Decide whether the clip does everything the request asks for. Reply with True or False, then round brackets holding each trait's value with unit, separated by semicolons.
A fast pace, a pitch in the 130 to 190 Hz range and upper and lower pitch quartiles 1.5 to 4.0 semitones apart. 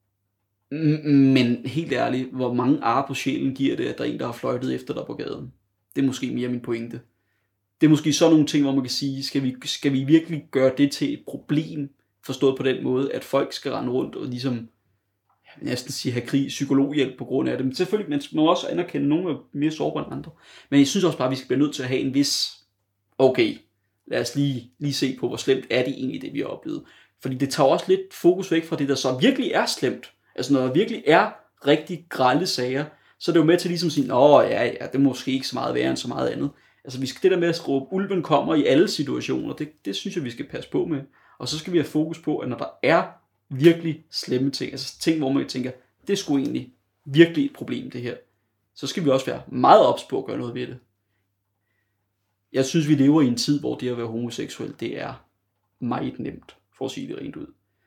True (250 wpm; 135 Hz; 3.6 semitones)